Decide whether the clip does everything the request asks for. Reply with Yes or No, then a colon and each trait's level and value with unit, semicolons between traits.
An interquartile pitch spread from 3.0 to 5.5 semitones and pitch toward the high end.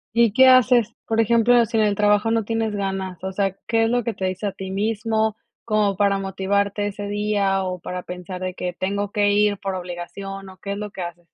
No: narrow, 2.4 semitones; high, 200 Hz